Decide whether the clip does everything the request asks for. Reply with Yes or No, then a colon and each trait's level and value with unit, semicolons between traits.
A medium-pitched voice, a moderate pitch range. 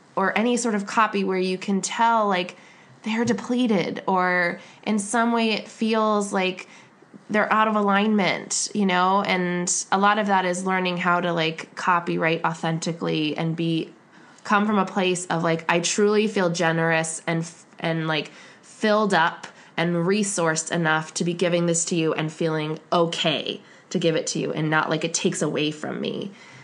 Yes: medium, 180 Hz; average, 3.8 semitones